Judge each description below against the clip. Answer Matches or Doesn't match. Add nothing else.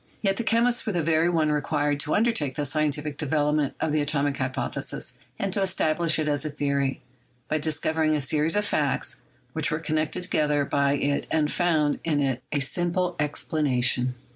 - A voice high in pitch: Doesn't match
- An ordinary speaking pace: Matches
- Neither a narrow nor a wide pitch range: Doesn't match